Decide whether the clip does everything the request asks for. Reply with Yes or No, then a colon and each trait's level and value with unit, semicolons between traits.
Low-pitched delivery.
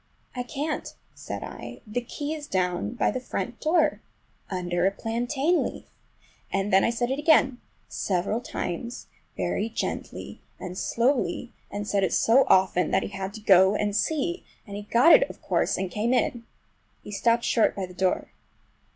No: high, 225 Hz